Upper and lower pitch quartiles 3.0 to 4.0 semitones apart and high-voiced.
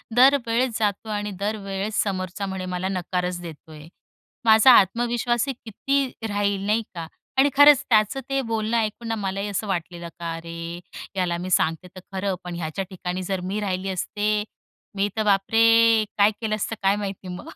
Yes: average, 3.4 semitones; high, 200 Hz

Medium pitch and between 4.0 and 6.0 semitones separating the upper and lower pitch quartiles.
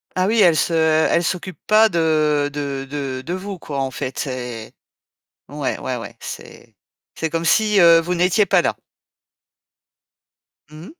Yes: medium, 160 Hz; average, 4.3 semitones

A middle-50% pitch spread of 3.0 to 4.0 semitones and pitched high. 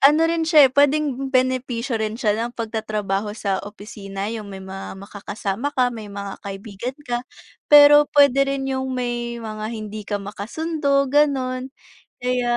No: average, 4.6 semitones; high, 240 Hz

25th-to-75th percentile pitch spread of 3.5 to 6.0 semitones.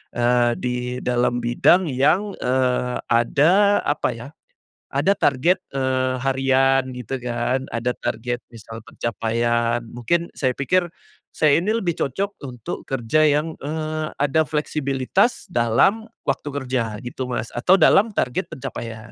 Yes: average, 4.2 semitones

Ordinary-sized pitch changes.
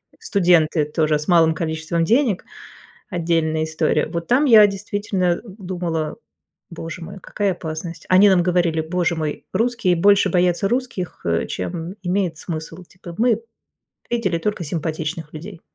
Yes: average, 3.4 semitones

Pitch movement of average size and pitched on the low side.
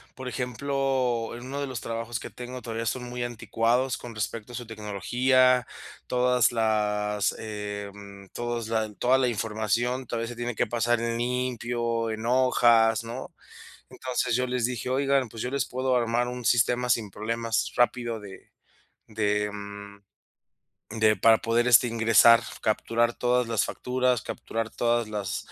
No: narrow, 2.1 semitones; low, 120 Hz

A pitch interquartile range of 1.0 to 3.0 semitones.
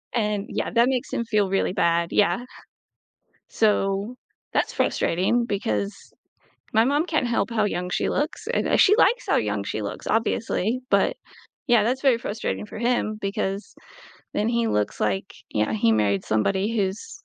No: average, 4.1 semitones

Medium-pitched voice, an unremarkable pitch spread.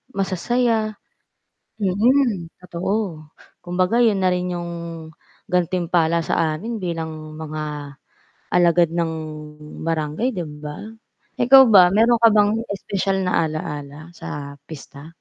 Yes: medium, 175 Hz; average, 4.2 semitones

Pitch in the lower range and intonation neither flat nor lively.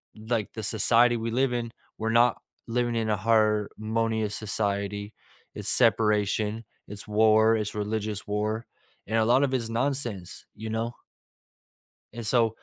No: low, 110 Hz; narrow, 1.6 semitones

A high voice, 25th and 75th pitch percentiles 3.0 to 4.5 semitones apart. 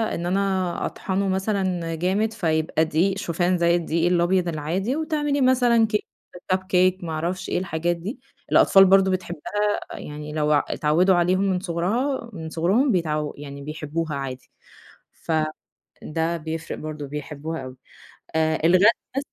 No: medium, 175 Hz; average, 3.5 semitones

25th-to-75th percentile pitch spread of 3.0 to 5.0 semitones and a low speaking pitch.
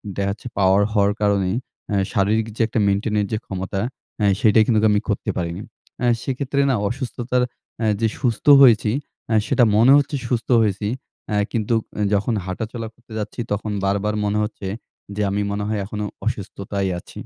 No: narrow, 2.4 semitones; low, 105 Hz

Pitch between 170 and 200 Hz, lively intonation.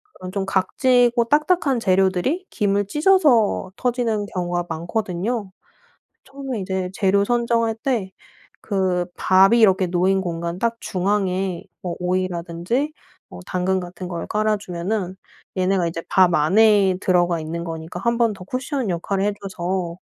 No: high, 190 Hz; average, 4.2 semitones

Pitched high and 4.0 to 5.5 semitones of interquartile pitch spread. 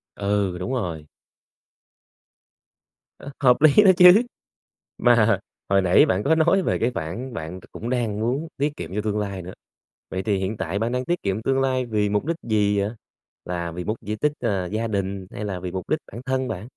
No: low, 105 Hz; average, 5.1 semitones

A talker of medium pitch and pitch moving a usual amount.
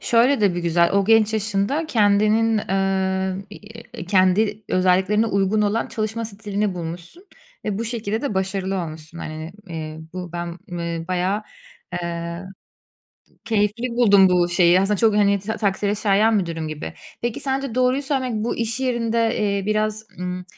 No: high, 200 Hz; average, 3.6 semitones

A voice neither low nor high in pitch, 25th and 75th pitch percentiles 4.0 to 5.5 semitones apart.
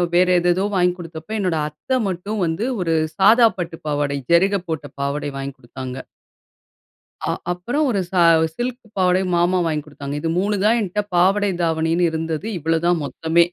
No: medium, 175 Hz; average, 3.4 semitones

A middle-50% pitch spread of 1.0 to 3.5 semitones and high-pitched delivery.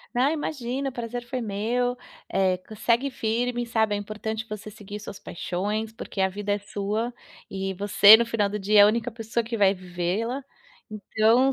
Yes: average, 2.7 semitones; high, 220 Hz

